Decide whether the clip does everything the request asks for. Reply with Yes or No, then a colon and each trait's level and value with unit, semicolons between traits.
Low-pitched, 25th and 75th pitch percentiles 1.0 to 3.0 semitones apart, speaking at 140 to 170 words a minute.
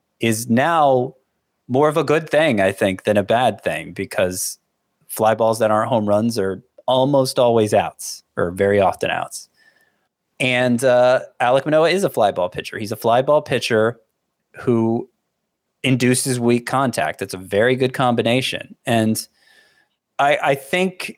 No: low, 125 Hz; average, 3.7 semitones; average, 155 wpm